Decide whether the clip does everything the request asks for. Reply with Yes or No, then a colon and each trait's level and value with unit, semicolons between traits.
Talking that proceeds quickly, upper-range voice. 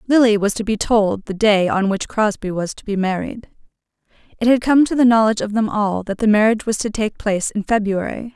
Yes: fast, 230 wpm; high, 215 Hz